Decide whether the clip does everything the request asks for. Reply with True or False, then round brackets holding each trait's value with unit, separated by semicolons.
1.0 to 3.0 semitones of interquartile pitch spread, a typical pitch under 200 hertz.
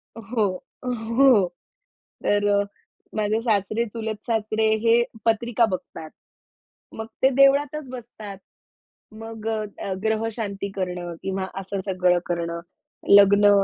False (2.6 semitones; 215 Hz)